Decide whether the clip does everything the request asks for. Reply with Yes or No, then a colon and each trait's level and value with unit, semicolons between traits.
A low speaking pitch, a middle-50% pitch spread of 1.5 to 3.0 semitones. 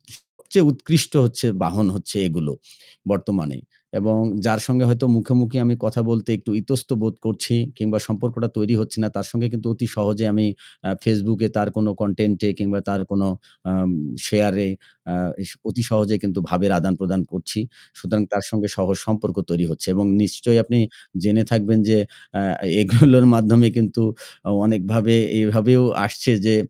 Yes: low, 110 Hz; average, 2.7 semitones